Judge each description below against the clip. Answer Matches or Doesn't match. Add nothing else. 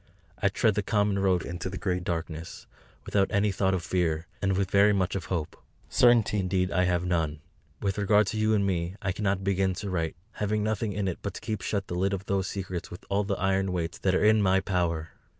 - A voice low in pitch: Matches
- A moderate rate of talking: Doesn't match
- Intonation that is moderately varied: Doesn't match